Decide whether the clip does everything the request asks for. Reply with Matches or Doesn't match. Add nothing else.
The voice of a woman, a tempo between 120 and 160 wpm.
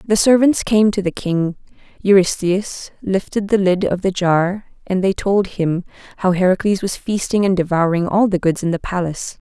Doesn't match